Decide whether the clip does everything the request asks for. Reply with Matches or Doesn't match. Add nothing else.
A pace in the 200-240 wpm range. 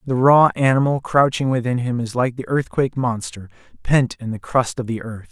Matches